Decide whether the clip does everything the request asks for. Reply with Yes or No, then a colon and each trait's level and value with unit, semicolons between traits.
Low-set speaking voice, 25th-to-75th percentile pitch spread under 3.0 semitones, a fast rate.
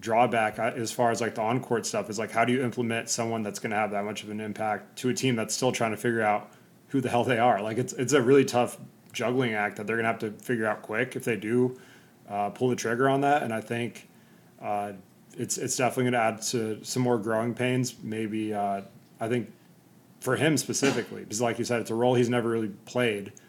Yes: low, 115 Hz; narrow, 2.5 semitones; fast, 250 wpm